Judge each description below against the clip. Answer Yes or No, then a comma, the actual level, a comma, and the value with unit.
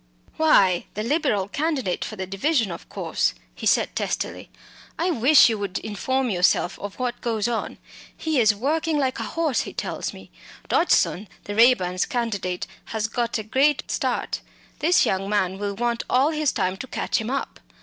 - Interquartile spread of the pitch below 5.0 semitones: No, wide, 5.4 semitones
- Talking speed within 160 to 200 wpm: Yes, average, 175 wpm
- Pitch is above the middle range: Yes, high, 230 Hz